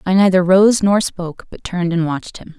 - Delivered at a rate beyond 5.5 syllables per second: Yes, 5.7 syllables/s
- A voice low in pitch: No, medium, 185 Hz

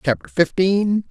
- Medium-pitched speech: Yes, medium, 175 Hz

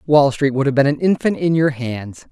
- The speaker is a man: Yes, male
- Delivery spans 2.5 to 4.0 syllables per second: No, 5.1 syllables/s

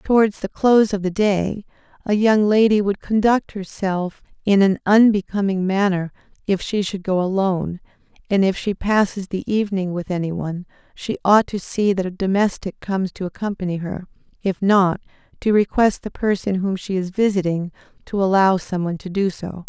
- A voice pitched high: Yes, high, 195 Hz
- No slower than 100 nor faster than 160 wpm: No, average, 175 wpm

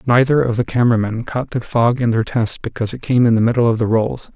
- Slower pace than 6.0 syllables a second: No, 6.2 syllables/s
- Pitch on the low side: Yes, low, 115 Hz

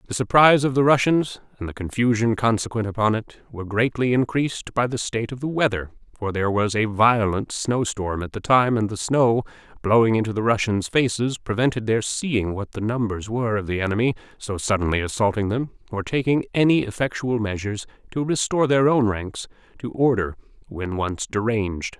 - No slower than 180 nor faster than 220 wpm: Yes, average, 185 wpm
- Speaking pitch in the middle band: No, low, 115 Hz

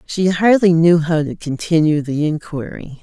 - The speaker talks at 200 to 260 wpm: No, average, 160 wpm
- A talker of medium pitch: Yes, medium, 165 Hz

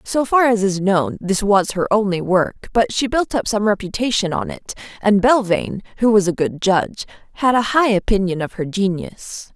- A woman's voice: Yes, female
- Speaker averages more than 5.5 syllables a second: No, 4.9 syllables/s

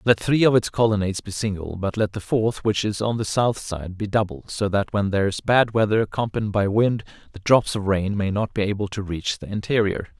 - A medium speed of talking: No, fast, 240 wpm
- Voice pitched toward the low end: Yes, low, 105 Hz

